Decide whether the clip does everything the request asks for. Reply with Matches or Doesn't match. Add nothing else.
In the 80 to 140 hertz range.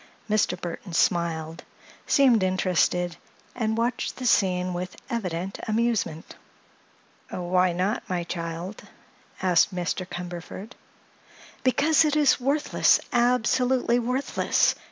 Doesn't match